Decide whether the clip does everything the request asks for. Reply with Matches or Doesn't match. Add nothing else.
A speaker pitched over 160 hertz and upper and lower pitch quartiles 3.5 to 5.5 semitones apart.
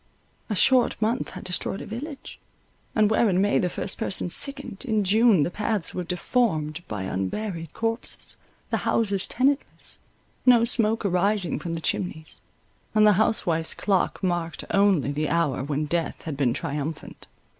Matches